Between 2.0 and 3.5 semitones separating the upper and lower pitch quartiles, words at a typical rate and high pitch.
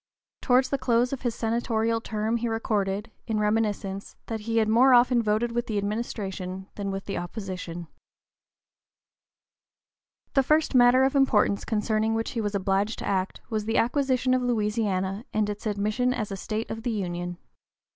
Yes: average, 2.9 semitones; average, 165 wpm; high, 220 Hz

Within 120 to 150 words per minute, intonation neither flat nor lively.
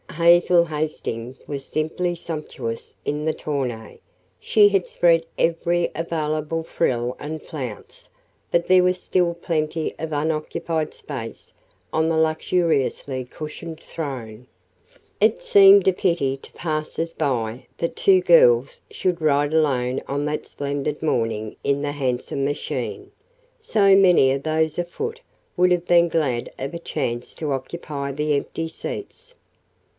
Yes: slow, 135 wpm; average, 3.6 semitones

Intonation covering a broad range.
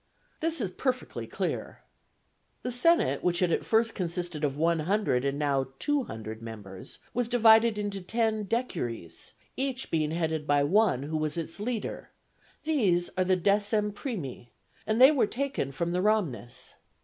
Yes: wide, 7.4 semitones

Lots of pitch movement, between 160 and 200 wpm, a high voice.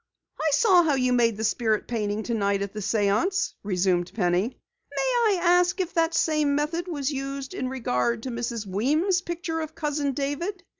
Yes: wide, 7.4 semitones; average, 180 wpm; very high, 275 Hz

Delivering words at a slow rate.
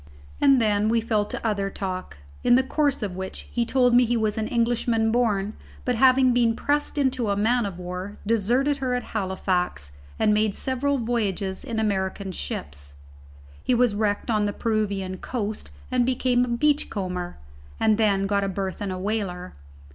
No: average, 175 wpm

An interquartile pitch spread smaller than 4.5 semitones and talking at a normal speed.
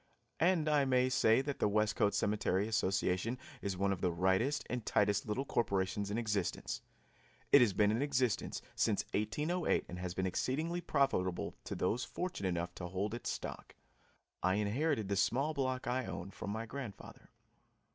No: average, 5.3 semitones; average, 165 wpm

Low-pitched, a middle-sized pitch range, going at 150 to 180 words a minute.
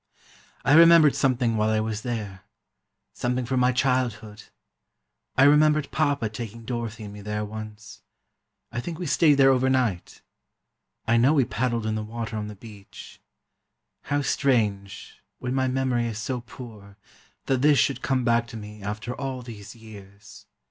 Yes: low, 120 Hz; average, 3.6 semitones; average, 160 wpm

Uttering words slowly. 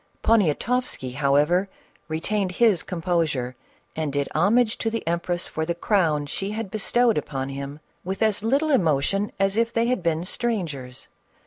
No: average, 150 wpm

